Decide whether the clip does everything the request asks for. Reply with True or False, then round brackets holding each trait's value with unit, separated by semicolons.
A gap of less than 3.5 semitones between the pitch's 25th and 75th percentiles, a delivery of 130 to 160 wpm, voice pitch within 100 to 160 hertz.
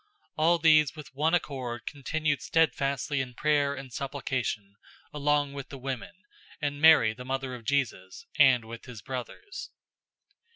True (3.0 semitones; 150 wpm; 140 Hz)